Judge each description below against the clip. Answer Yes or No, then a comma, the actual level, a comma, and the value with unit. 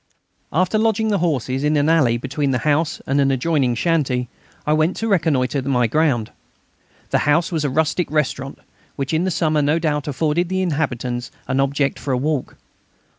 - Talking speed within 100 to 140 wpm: No, average, 180 wpm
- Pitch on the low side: No, medium, 150 Hz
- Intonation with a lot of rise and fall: No, average, 3.6 semitones